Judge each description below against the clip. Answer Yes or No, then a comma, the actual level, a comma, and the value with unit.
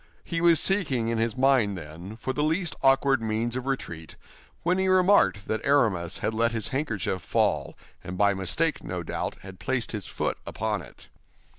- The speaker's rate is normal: Yes, average, 180 wpm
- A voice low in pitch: Yes, low, 115 Hz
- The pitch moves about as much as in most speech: No, wide, 6.4 semitones